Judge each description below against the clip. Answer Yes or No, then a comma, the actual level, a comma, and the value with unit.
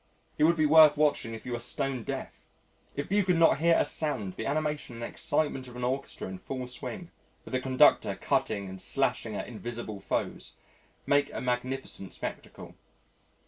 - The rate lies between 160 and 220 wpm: Yes, average, 180 wpm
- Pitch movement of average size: Yes, average, 4.3 semitones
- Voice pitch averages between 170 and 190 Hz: No, low, 130 Hz